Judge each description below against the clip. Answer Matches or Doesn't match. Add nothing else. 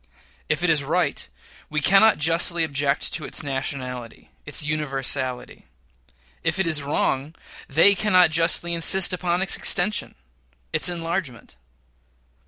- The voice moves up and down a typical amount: Matches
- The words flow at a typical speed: Doesn't match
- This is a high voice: Doesn't match